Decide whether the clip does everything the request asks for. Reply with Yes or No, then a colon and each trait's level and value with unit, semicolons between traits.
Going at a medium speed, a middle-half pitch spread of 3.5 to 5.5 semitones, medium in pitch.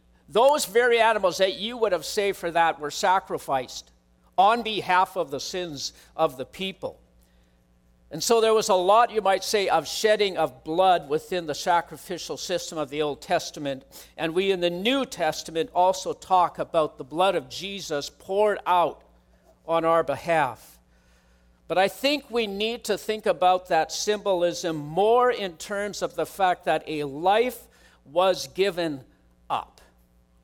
Yes: average, 160 wpm; average, 5.0 semitones; medium, 175 Hz